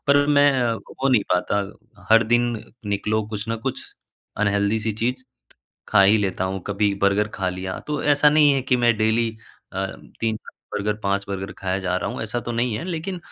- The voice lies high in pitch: No, low, 110 Hz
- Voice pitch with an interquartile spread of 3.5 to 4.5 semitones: Yes, average, 4.1 semitones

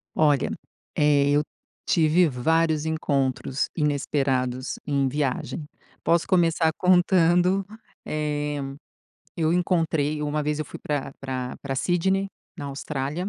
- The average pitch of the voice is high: No, medium, 150 Hz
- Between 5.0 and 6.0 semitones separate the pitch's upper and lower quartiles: No, average, 3.0 semitones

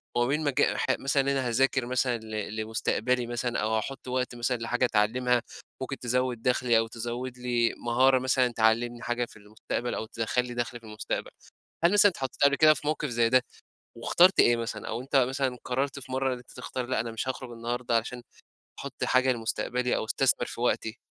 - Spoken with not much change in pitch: Yes, narrow, 1.9 semitones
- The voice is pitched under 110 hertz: No, low, 125 Hz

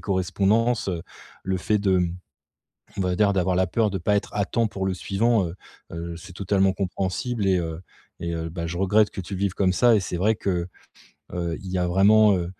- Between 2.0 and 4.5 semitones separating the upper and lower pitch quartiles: Yes, narrow, 2.6 semitones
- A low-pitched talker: Yes, very low, 95 Hz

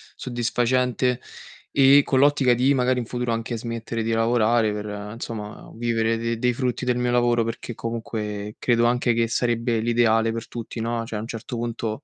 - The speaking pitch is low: Yes, low, 115 Hz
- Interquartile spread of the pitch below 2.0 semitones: Yes, narrow, 1.4 semitones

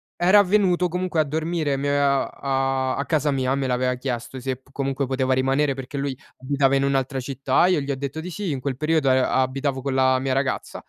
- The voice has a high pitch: No, low, 135 Hz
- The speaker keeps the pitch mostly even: Yes, narrow, 2.1 semitones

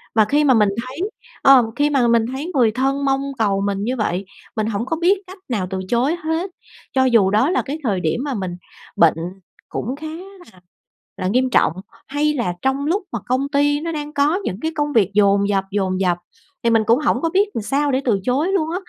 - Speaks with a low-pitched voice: No, very high, 255 Hz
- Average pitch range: No, wide, 6.0 semitones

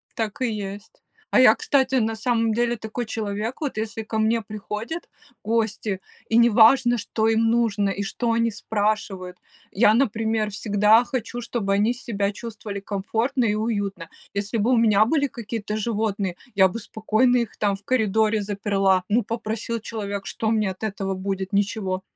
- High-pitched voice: Yes, high, 220 Hz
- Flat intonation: Yes, narrow, 2.2 semitones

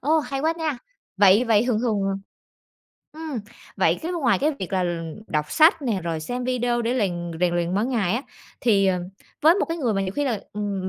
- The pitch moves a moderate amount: No, wide, 6.3 semitones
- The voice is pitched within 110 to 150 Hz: No, high, 230 Hz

